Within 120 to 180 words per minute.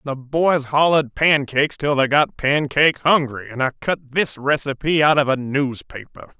Yes: average, 170 wpm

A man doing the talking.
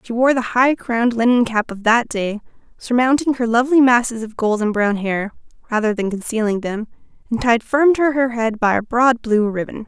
No: female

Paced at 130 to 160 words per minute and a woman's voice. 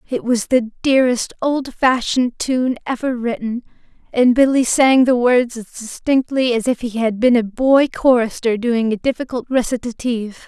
Yes: average, 155 wpm; female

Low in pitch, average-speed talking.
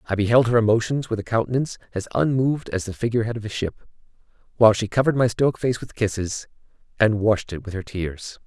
No: low, 110 Hz; fast, 215 wpm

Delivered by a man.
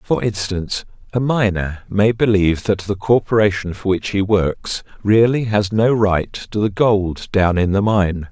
Yes: male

